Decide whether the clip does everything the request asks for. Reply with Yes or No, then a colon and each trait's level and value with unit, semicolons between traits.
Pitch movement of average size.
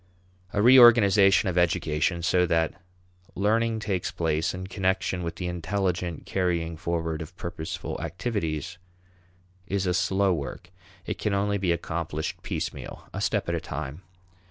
Yes: average, 3.0 semitones